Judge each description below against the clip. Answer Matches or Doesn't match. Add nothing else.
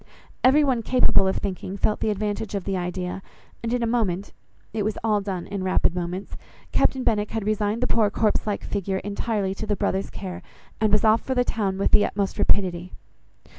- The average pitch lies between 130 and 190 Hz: Doesn't match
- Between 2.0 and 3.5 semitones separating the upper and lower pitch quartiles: Matches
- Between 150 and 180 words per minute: Doesn't match